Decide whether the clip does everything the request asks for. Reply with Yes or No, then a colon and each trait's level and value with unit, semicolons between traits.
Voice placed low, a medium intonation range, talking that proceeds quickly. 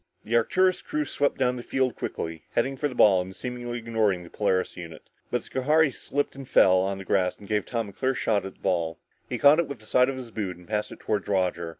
No: low, 110 Hz; wide, 5.7 semitones; fast, 250 wpm